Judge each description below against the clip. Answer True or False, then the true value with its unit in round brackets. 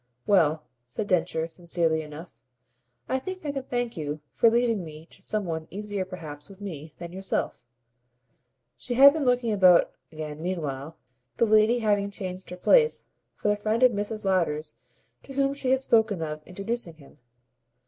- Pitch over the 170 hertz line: True (190 Hz)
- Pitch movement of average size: False (6.1 semitones)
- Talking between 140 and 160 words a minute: False (170 wpm)